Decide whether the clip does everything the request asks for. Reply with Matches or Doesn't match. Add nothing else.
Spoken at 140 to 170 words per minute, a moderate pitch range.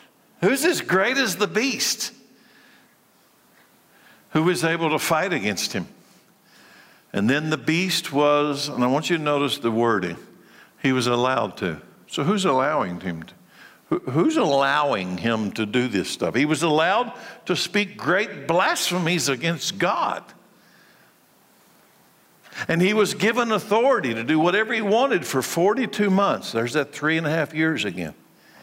Doesn't match